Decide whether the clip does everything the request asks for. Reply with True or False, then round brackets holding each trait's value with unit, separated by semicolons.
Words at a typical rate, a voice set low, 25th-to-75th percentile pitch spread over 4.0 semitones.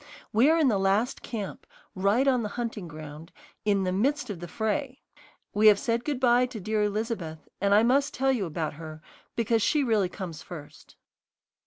False (190 wpm; 215 Hz; 4.9 semitones)